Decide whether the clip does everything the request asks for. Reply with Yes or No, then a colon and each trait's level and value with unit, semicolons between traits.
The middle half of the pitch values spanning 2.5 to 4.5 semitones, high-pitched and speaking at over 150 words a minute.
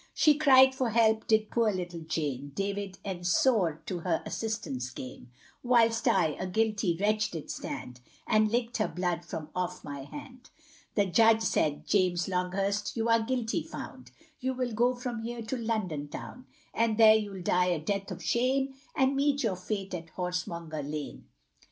No: average, 4.9 semitones; high, 205 Hz; average, 170 wpm